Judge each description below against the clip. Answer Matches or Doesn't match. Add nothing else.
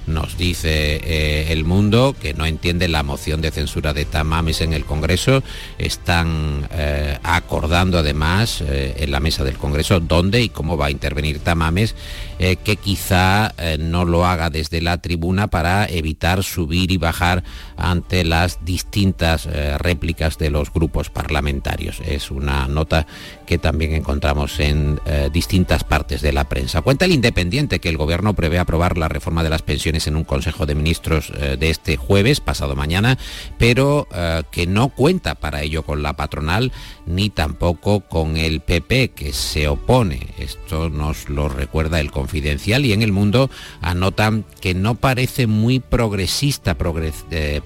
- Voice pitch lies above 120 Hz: Doesn't match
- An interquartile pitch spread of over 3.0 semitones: Matches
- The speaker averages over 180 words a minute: Doesn't match